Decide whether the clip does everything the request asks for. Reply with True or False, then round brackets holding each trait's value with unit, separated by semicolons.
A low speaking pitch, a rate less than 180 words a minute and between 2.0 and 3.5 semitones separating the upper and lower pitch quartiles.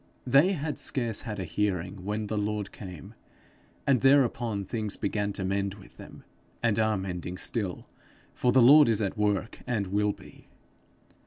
True (105 Hz; 165 wpm; 3.2 semitones)